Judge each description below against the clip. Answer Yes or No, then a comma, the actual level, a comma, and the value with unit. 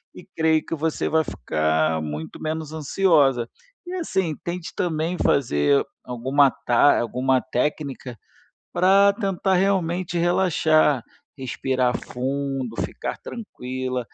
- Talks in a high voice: No, medium, 145 Hz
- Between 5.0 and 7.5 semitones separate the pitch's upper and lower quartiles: Yes, wide, 5.6 semitones